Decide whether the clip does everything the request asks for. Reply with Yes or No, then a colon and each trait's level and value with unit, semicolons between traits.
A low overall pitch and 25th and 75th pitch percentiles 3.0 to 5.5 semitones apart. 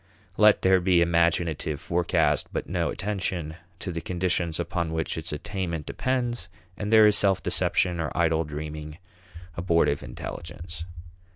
No: very low, 85 Hz; narrow, 2.6 semitones